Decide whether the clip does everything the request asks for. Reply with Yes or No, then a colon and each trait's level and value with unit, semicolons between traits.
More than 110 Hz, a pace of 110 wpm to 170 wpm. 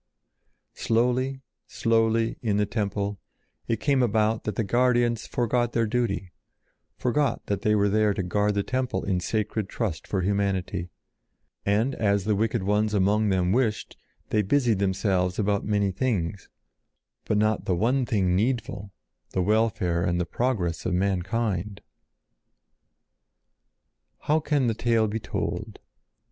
No: low, 105 Hz; average, 140 wpm